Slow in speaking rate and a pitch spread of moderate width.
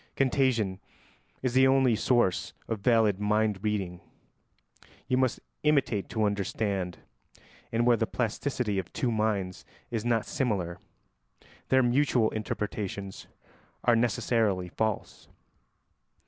Yes: slow, 110 wpm; average, 3.4 semitones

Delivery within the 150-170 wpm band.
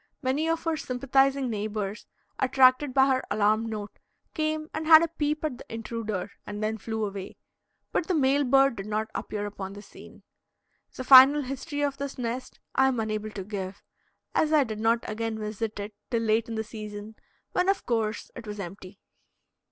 No: average, 185 wpm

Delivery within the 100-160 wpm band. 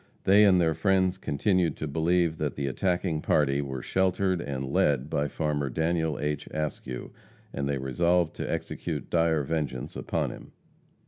Yes: average, 155 wpm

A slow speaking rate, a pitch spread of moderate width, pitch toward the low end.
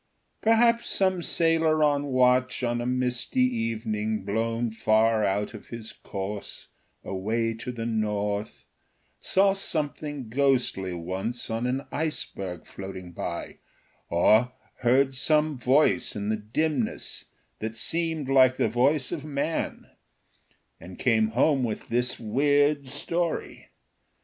Yes: slow, 120 wpm; average, 4.9 semitones; low, 125 Hz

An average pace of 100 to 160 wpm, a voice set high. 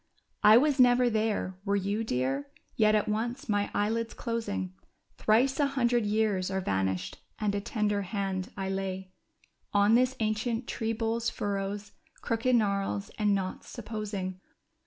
Yes: average, 145 wpm; high, 210 Hz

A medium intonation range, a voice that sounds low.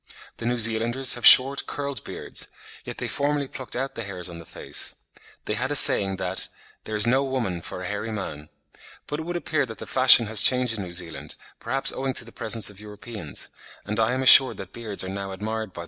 Yes: average, 4.9 semitones; low, 115 Hz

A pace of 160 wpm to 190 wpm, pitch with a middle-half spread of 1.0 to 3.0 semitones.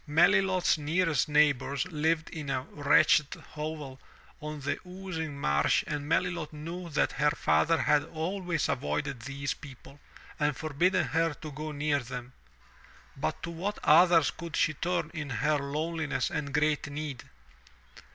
No: average, 140 wpm; narrow, 2.5 semitones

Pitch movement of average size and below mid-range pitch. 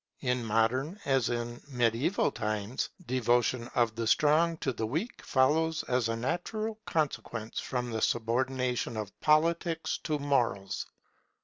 Yes: average, 4.8 semitones; low, 125 Hz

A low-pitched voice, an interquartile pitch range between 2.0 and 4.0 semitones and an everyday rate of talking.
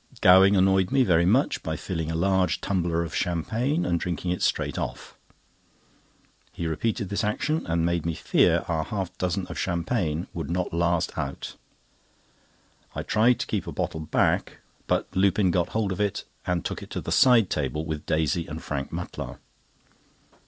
Yes: very low, 90 Hz; average, 3.1 semitones; average, 175 wpm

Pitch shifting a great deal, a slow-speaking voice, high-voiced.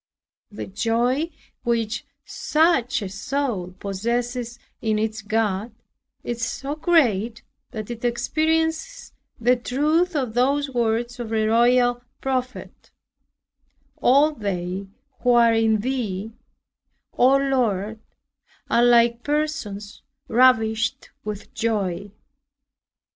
No: average, 3.3 semitones; slow, 100 wpm; high, 235 Hz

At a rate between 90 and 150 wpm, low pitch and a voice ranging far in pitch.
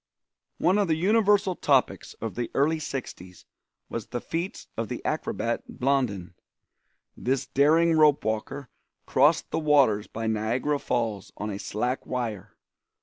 Yes: average, 140 wpm; low, 130 Hz; wide, 6.0 semitones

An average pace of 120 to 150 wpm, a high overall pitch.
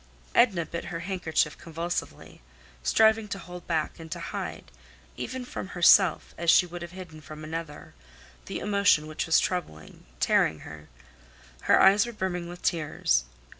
No: average, 145 wpm; medium, 170 Hz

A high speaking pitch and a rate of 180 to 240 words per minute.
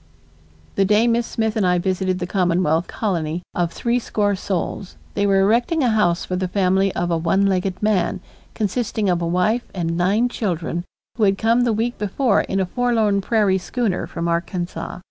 Yes: high, 195 Hz; average, 185 wpm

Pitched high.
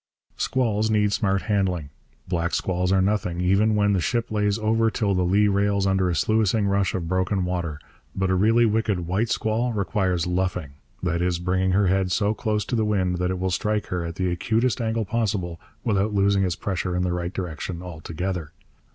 No: very low, 95 Hz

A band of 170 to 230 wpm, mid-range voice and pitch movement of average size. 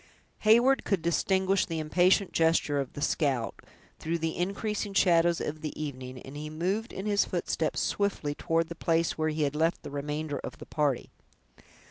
Yes: average, 175 wpm; medium, 165 Hz; average, 4.2 semitones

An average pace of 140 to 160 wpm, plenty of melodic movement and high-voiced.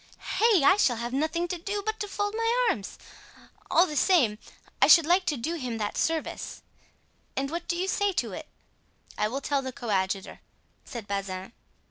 No: average, 175 wpm; wide, 8.3 semitones; very high, 310 Hz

